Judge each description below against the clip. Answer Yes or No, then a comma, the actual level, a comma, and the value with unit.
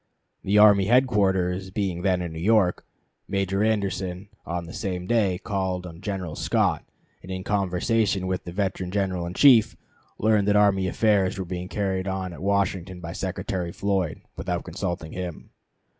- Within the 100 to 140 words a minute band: No, average, 160 wpm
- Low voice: Yes, very low, 95 Hz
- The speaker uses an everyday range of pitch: No, narrow, 2.1 semitones